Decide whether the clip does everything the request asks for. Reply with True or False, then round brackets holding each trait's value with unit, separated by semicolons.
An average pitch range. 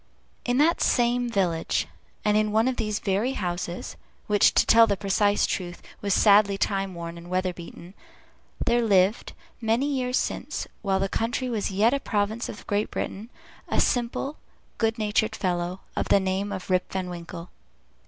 True (3.5 semitones)